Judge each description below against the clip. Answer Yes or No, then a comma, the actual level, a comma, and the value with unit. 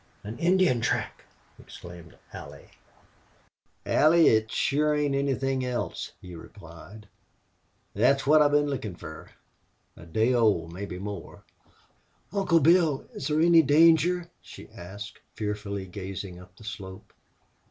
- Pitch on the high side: No, low, 120 Hz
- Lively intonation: Yes, wide, 7.4 semitones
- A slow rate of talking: Yes, slow, 130 wpm